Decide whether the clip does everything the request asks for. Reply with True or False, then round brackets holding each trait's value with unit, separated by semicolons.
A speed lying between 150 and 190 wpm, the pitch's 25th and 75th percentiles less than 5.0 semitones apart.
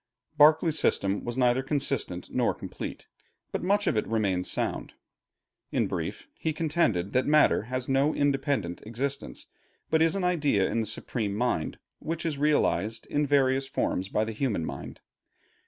False (155 wpm; 5.5 semitones)